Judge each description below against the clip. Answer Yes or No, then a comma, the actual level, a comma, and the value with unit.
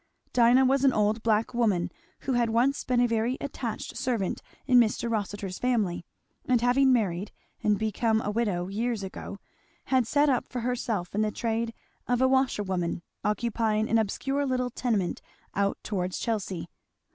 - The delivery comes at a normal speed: Yes, average, 160 wpm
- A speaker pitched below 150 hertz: No, high, 230 Hz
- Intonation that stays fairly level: No, average, 3.2 semitones